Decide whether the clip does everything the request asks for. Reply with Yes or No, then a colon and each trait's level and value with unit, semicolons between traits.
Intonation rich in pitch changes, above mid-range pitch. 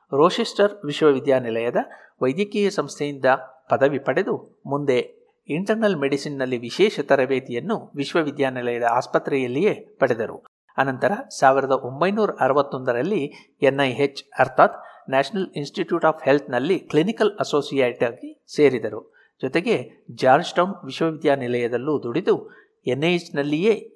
No: wide, 6.3 semitones; medium, 145 Hz